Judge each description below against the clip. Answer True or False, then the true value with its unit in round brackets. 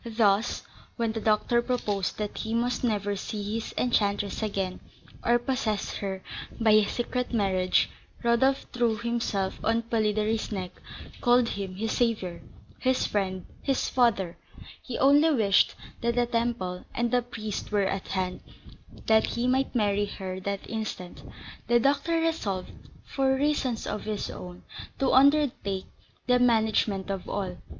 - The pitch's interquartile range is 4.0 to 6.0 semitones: False (3.5 semitones)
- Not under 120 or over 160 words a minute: True (145 wpm)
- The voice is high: True (220 Hz)